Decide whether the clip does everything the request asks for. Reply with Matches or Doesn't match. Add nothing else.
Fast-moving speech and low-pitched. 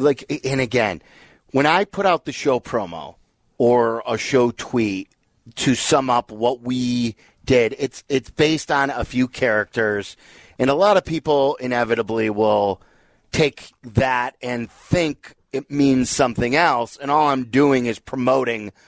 Doesn't match